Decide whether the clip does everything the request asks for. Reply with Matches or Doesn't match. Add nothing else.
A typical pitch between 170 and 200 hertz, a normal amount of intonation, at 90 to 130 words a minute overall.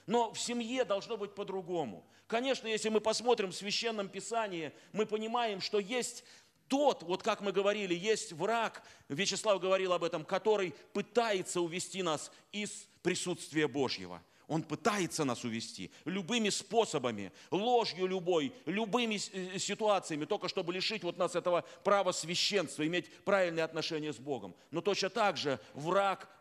Doesn't match